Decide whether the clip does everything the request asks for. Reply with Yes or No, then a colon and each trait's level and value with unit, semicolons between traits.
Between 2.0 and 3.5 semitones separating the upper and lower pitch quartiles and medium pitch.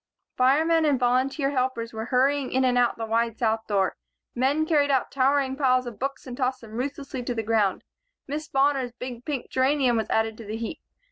No: average, 3.1 semitones; very high, 255 Hz